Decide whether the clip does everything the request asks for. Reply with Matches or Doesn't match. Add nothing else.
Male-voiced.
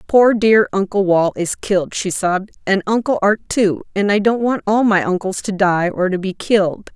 Doesn't match